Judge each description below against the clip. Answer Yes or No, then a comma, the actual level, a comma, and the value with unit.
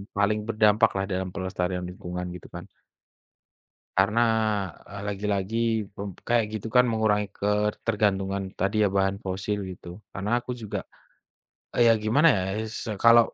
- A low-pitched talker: Yes, low, 105 Hz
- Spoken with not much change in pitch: Yes, narrow, 2.3 semitones